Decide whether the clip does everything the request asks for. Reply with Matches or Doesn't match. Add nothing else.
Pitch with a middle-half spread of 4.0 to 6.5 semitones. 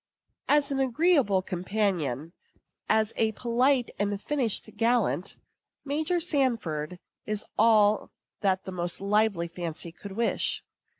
Matches